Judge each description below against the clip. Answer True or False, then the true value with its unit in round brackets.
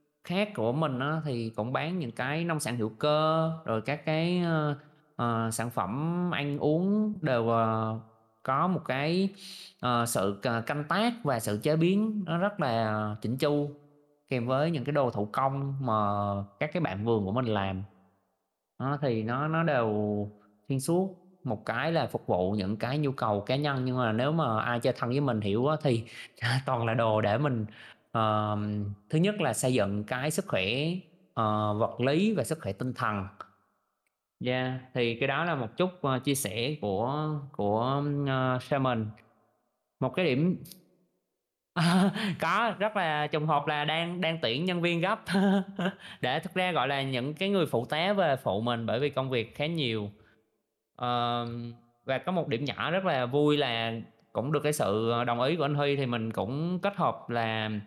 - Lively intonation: True (5.7 semitones)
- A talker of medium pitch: False (130 Hz)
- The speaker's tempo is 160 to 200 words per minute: True (180 wpm)